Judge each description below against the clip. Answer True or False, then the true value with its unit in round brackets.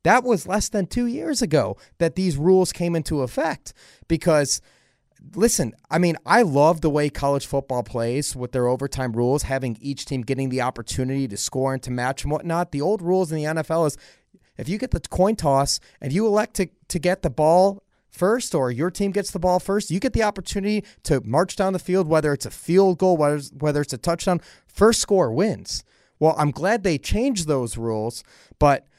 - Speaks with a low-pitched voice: False (160 Hz)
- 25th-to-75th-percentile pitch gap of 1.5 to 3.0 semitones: False (5.5 semitones)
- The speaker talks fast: True (210 wpm)